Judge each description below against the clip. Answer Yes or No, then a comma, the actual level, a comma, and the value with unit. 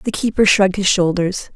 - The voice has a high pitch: Yes, high, 195 Hz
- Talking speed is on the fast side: No, average, 195 wpm